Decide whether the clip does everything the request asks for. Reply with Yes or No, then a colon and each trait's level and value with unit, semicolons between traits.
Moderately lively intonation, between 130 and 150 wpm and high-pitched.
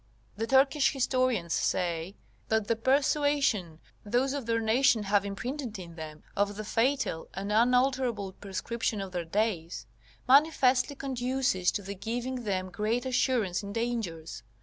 Yes: average, 5.0 semitones; average, 140 wpm; high, 225 Hz